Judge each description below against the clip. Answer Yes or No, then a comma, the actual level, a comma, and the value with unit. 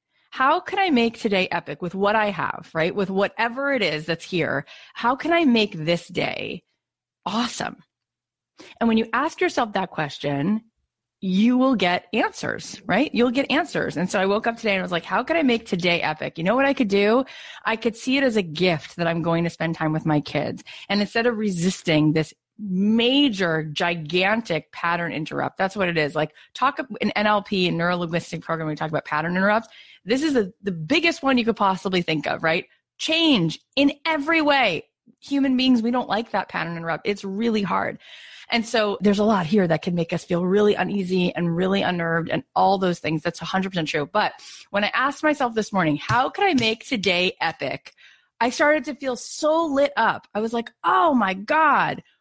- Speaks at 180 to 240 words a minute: Yes, fast, 205 wpm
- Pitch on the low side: No, high, 200 Hz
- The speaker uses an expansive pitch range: Yes, wide, 6.3 semitones